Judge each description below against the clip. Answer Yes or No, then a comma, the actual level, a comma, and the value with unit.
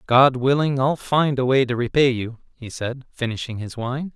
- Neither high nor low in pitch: No, low, 130 Hz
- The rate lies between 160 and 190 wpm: No, average, 200 wpm